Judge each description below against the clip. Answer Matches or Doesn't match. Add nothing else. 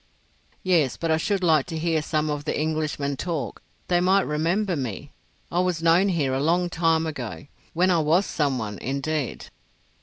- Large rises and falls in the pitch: Doesn't match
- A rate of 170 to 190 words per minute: Matches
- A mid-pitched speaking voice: Matches